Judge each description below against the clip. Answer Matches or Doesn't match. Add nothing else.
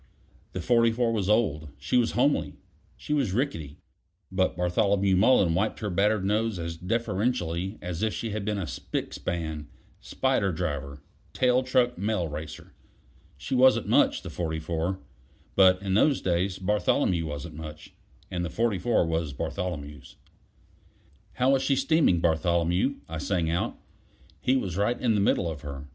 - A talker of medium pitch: Doesn't match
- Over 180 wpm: Doesn't match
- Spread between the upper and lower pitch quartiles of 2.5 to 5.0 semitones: Doesn't match